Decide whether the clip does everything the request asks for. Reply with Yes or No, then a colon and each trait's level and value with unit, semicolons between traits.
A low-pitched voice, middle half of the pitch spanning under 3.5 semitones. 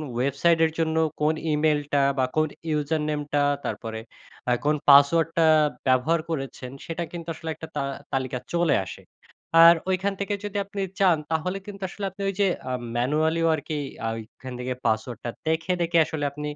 No: medium, 155 Hz; average, 3.1 semitones